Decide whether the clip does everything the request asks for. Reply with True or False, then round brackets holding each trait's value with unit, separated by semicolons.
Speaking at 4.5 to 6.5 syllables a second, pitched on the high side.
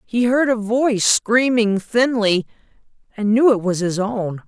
False (4.2 syllables/s; 220 Hz)